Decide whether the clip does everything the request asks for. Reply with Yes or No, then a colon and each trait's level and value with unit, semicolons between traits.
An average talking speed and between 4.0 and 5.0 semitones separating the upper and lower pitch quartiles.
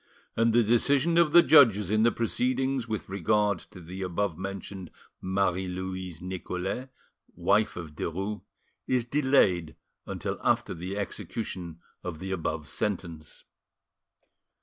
No: slow, 125 wpm; average, 4.4 semitones